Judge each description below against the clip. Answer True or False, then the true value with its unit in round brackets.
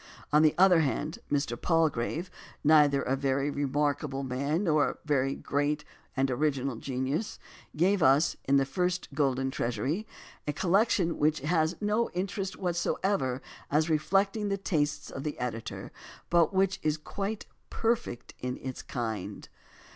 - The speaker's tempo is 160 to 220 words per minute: False (145 wpm)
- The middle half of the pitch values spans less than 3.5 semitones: False (4.8 semitones)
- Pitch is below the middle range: False (150 Hz)